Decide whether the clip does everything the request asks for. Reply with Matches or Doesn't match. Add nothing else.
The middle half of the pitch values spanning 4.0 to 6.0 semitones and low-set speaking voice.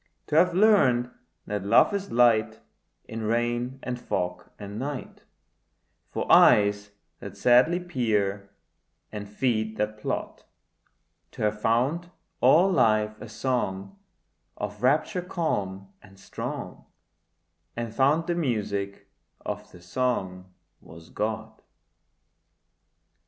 Matches